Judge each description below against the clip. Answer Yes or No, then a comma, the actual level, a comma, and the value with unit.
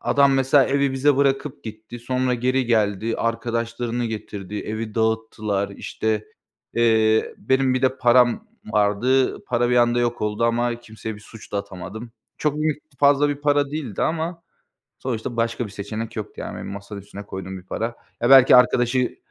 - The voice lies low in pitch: Yes, low, 120 Hz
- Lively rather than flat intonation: No, average, 3.2 semitones